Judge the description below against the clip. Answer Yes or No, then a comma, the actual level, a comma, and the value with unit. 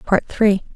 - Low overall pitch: No, high, 200 Hz